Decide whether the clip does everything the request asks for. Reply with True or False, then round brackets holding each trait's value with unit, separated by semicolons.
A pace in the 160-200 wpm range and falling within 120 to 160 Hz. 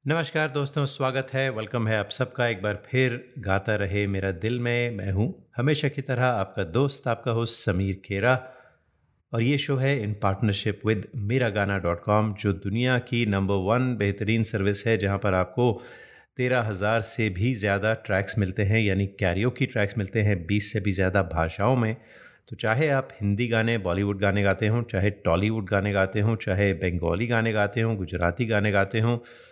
False (185 wpm; 110 Hz)